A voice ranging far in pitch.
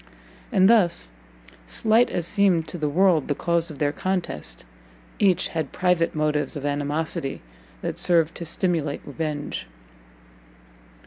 No: average, 3.7 semitones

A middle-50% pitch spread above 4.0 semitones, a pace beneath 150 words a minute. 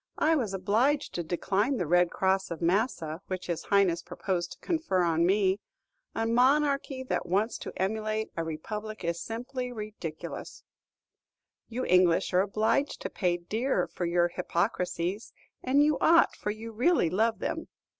No: average, 5.0 semitones; average, 155 wpm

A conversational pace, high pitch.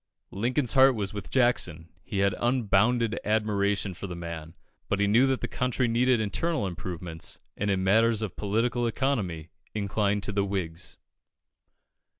No: average, 150 wpm; low, 105 Hz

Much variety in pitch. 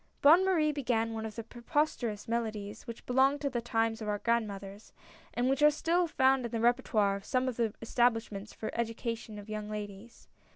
No: average, 3.4 semitones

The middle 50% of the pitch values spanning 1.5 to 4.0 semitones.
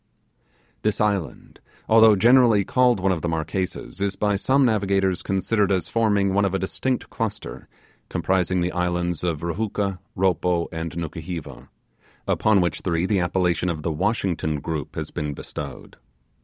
Yes: average, 3.3 semitones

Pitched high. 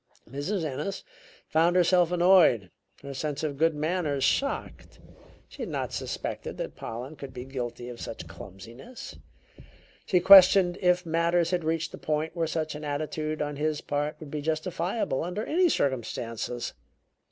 No: medium, 155 Hz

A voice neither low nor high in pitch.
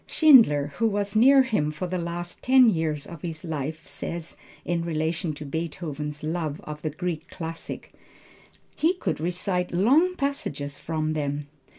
Yes: medium, 165 Hz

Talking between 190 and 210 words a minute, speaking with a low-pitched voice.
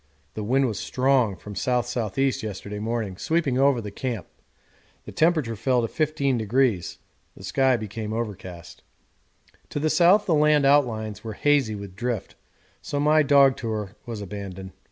No: average, 155 wpm; low, 120 Hz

